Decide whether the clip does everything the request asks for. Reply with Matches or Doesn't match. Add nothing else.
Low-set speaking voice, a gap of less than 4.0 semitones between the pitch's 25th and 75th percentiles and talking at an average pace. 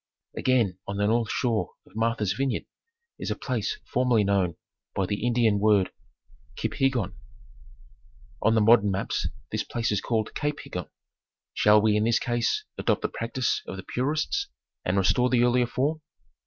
Matches